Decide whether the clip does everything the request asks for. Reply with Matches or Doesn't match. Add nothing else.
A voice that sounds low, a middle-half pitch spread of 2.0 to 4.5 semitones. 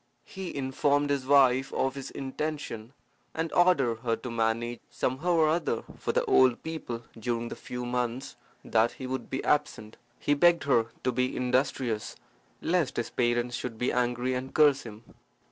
Matches